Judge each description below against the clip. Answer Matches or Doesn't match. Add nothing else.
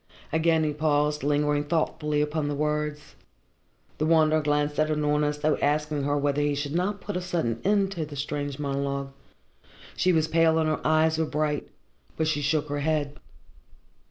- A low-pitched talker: Doesn't match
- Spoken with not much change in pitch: Matches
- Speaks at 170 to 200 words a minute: Matches